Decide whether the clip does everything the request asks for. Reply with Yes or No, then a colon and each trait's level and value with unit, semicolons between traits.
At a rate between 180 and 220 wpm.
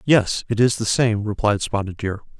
Yes: average, 200 wpm